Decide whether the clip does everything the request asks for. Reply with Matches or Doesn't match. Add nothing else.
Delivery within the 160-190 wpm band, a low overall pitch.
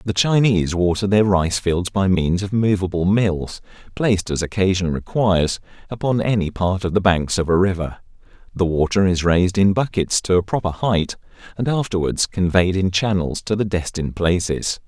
Matches